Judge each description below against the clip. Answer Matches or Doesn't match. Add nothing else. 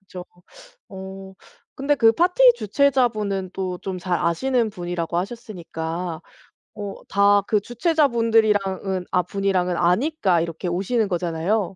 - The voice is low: Doesn't match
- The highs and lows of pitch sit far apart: Doesn't match